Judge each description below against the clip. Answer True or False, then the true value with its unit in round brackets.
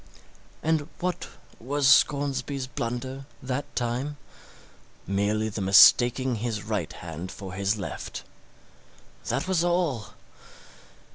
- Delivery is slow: True (100 wpm)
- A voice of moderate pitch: False (125 Hz)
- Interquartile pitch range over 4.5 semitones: True (5.3 semitones)